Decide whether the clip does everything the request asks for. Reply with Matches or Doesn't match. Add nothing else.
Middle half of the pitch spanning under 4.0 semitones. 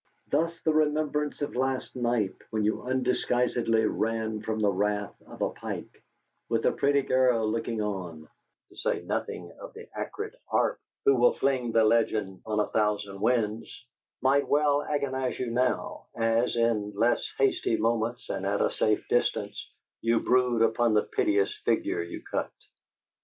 Matches